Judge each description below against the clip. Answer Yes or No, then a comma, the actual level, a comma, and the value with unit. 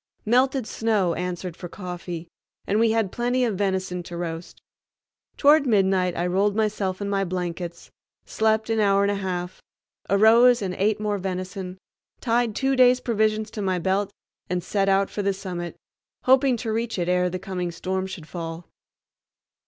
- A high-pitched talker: Yes, high, 195 Hz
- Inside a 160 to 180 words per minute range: Yes, average, 170 wpm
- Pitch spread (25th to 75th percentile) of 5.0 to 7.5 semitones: No, average, 3.3 semitones